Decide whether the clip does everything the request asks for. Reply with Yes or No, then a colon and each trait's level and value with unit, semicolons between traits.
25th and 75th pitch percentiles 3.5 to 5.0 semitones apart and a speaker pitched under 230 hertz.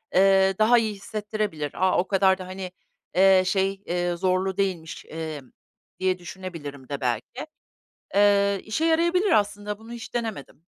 No: average, 2.8 semitones; high, 190 Hz